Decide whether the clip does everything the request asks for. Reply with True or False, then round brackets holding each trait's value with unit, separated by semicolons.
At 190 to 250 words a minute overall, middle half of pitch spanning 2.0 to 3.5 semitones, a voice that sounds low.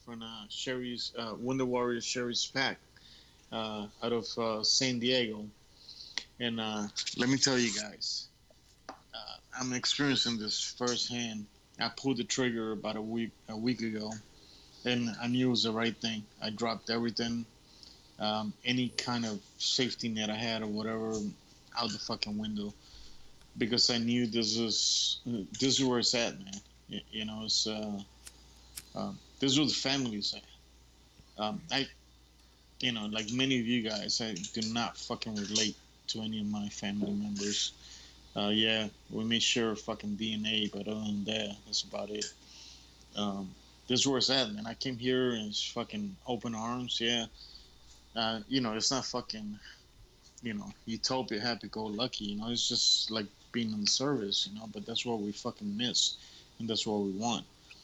False (175 wpm; 2.8 semitones; 110 Hz)